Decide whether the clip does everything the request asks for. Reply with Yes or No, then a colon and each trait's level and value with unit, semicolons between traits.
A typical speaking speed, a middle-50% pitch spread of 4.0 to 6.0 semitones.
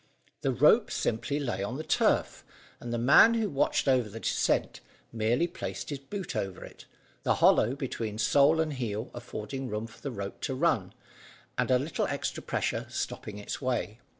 Yes: average, 180 wpm; average, 4.6 semitones